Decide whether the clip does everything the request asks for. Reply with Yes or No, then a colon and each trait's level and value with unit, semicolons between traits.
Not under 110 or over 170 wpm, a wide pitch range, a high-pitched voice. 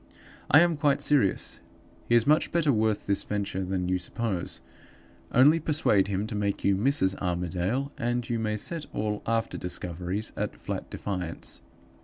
No: average, 160 wpm; wide, 5.8 semitones; low, 105 Hz